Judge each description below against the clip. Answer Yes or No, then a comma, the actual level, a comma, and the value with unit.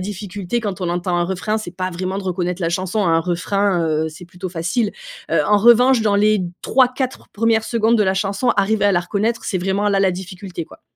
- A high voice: Yes, high, 195 Hz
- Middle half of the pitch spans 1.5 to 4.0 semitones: Yes, average, 3.1 semitones